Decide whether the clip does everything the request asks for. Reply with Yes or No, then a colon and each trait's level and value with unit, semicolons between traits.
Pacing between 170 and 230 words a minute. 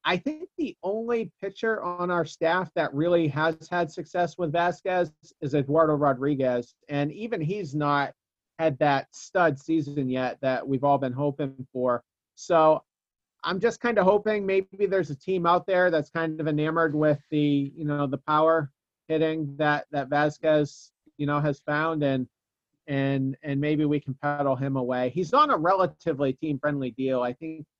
Yes: average, 175 wpm